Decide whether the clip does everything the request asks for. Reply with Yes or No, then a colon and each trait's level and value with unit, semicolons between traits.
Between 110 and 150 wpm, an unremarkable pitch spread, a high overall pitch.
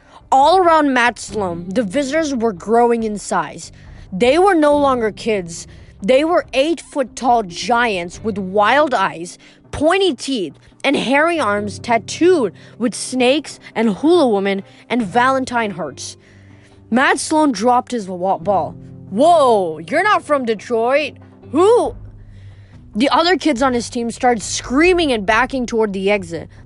No: average, 140 wpm; wide, 6.4 semitones; high, 235 Hz